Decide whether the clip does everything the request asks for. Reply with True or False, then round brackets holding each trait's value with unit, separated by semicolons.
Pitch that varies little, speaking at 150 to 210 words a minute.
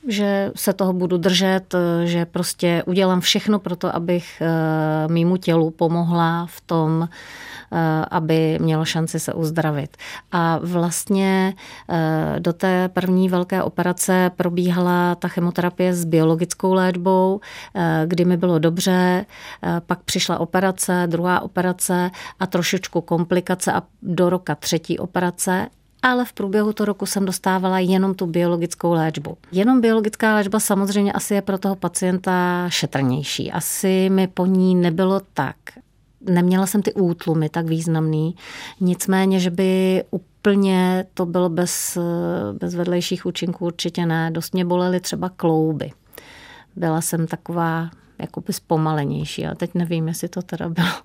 False (2.0 semitones; 135 wpm)